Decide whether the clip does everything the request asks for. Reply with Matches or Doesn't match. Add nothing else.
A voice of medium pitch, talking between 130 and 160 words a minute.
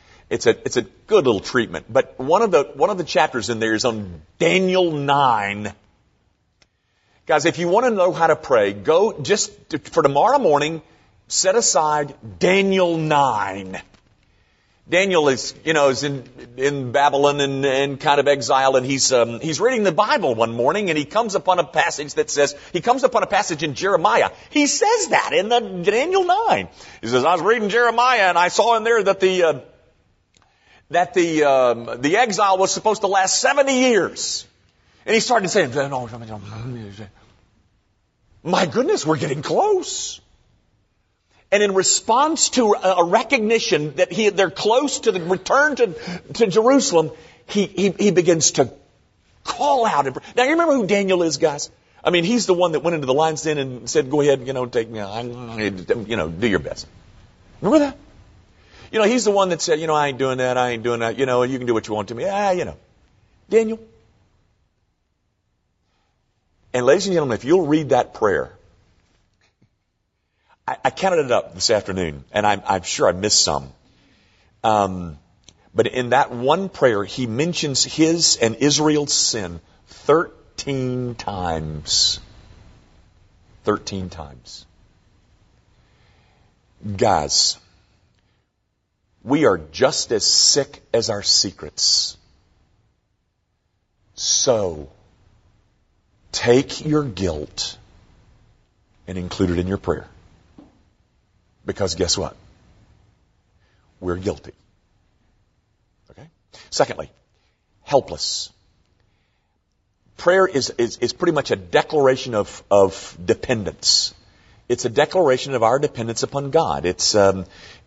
Doesn't match